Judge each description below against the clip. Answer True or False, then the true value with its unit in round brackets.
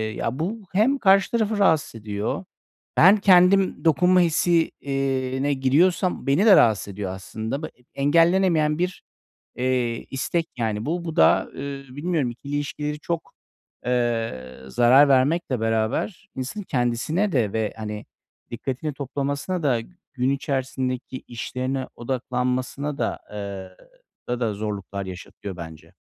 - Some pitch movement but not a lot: False (6.1 semitones)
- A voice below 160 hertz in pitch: True (135 Hz)